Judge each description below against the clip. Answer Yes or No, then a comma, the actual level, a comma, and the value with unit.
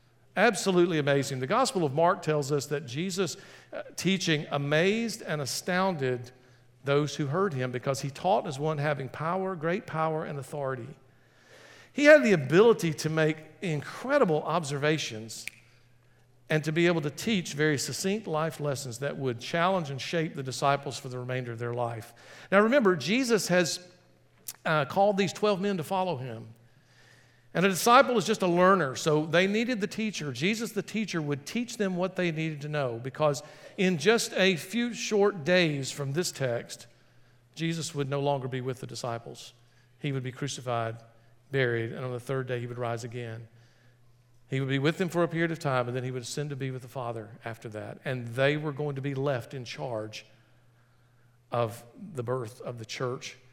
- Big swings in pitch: Yes, wide, 6.0 semitones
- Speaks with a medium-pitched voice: Yes, medium, 145 Hz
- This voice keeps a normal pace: Yes, average, 185 wpm